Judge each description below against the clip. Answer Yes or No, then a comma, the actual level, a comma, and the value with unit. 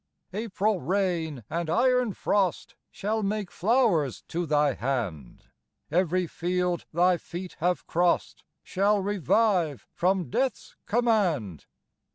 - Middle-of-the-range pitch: Yes, medium, 180 Hz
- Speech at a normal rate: No, slow, 110 wpm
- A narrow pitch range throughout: No, average, 4.2 semitones